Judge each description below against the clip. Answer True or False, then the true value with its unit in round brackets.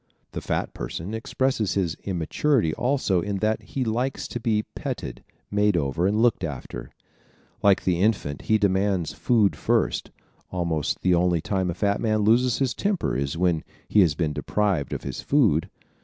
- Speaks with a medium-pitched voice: False (100 Hz)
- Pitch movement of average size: True (4.7 semitones)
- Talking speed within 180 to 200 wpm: False (170 wpm)